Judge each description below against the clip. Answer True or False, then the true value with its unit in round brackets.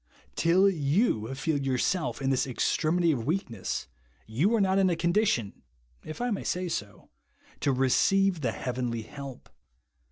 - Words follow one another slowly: False (150 wpm)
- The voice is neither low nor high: True (150 Hz)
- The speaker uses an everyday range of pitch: False (6.4 semitones)